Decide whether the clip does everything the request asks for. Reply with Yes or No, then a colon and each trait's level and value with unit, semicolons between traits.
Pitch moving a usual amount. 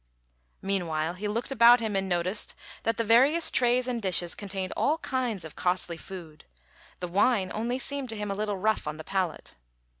Yes: average, 4.6 semitones